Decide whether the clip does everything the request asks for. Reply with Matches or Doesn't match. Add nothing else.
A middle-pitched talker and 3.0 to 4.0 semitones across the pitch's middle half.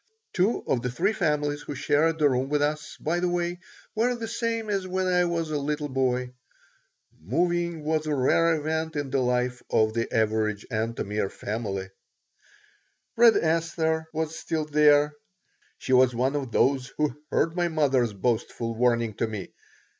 Doesn't match